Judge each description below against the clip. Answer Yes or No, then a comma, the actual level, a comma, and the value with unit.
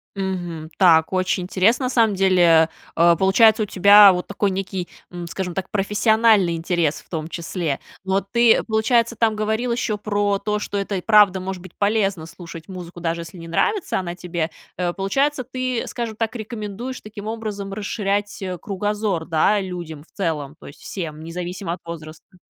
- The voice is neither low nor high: No, high, 195 Hz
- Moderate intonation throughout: Yes, average, 3.6 semitones